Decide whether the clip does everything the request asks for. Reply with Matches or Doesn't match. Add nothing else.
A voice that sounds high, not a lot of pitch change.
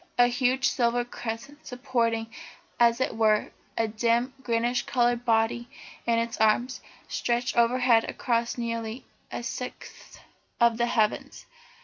Matches